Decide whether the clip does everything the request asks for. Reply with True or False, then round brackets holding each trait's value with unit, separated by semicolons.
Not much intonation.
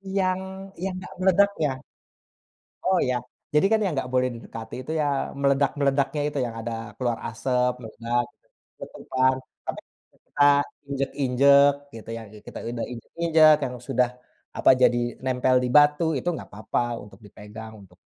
False (3.7 semitones)